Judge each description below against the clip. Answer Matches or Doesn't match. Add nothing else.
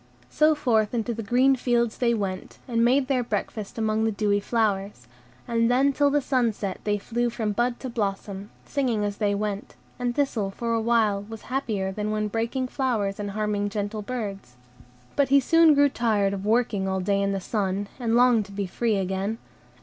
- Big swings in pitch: Doesn't match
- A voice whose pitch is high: Matches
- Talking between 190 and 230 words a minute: Matches